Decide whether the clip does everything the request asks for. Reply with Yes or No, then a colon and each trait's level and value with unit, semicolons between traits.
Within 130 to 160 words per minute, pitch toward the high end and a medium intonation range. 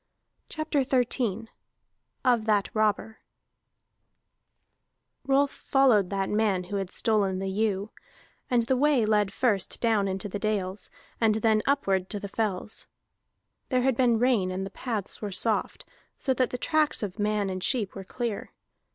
Yes: average, 150 wpm; high, 215 Hz; average, 3.9 semitones